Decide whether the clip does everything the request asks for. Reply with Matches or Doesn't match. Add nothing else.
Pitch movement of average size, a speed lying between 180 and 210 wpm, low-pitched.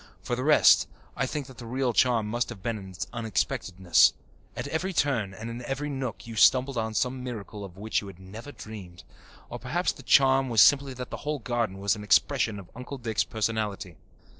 Matches